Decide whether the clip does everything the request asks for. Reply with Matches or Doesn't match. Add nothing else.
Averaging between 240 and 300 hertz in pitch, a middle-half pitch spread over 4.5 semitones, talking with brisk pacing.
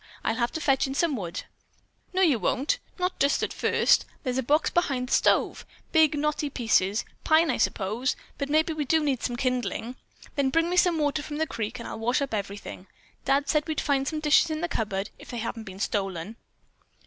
Matches